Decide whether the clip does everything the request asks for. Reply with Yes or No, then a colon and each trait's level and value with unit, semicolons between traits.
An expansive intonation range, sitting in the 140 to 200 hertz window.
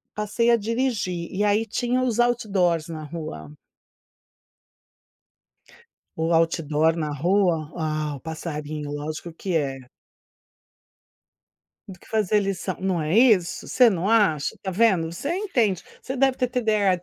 Yes: wide, 5.7 semitones; medium, 185 Hz